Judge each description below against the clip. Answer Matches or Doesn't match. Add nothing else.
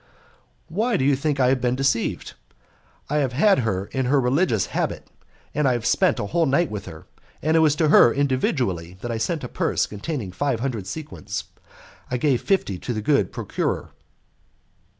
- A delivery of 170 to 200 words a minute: Matches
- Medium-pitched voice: Doesn't match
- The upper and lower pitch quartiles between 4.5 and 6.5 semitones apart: Matches